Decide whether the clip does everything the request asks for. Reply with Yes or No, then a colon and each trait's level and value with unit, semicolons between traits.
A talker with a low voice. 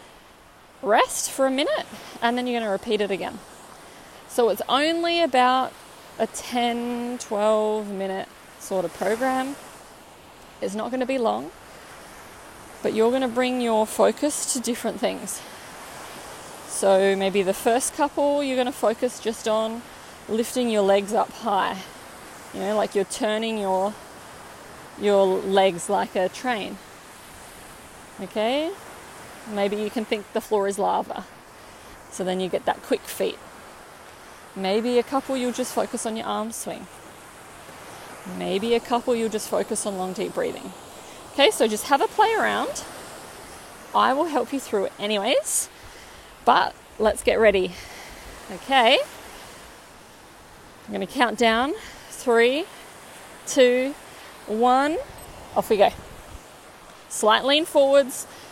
No: high, 230 Hz